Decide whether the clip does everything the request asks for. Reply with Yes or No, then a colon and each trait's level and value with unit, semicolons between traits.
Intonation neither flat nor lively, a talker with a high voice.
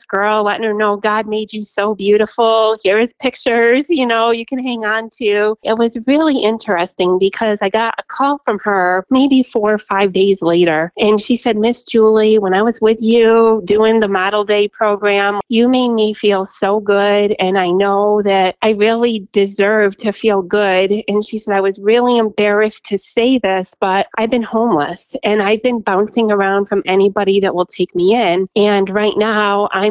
No: narrow, 2.3 semitones; high, 210 Hz